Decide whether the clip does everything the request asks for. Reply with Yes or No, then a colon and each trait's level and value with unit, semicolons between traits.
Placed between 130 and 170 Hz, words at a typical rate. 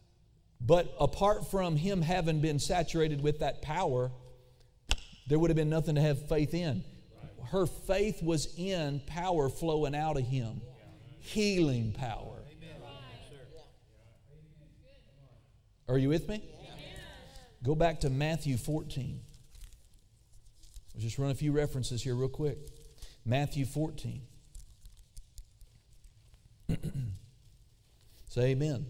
No: medium, 140 Hz; slow, 110 wpm